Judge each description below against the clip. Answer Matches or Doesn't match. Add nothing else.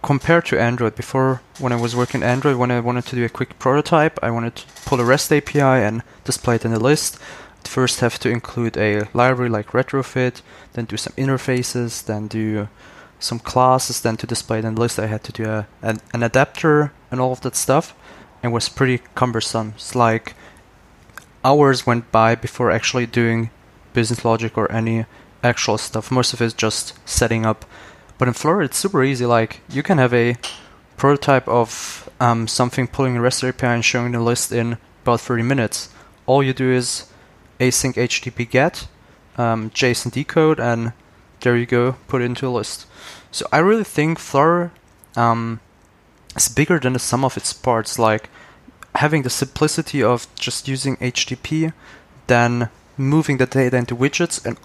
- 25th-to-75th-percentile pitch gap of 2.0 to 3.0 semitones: Matches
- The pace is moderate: Matches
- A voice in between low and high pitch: Doesn't match